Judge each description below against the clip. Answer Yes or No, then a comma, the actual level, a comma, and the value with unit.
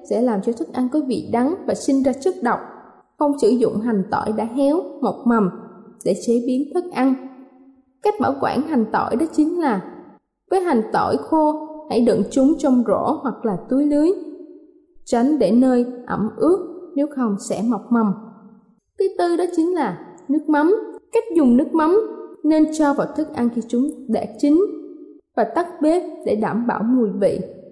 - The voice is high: Yes, very high, 270 Hz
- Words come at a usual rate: Yes, average, 185 wpm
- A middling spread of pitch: No, wide, 5.8 semitones